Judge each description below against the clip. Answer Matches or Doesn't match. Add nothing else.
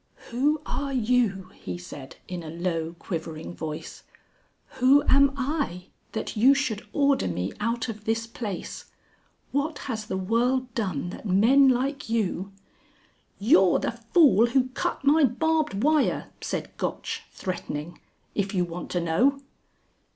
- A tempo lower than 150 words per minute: Matches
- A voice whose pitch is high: Matches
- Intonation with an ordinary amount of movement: Doesn't match